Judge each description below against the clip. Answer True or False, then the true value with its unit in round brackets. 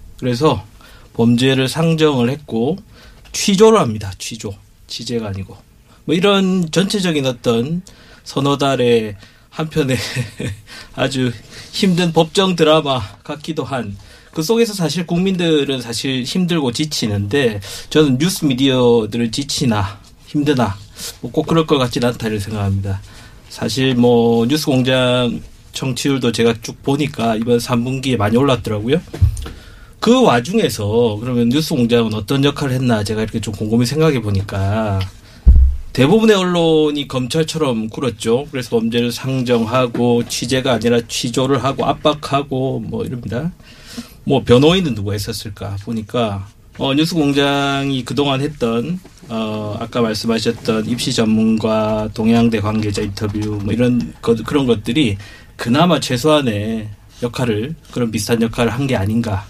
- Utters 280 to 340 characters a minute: True (295 characters per minute)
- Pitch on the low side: True (120 Hz)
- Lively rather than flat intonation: False (4.4 semitones)